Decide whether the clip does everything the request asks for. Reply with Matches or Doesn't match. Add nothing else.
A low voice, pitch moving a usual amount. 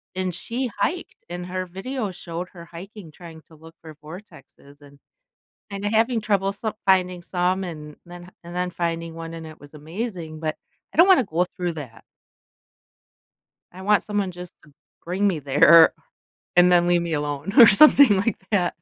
Doesn't match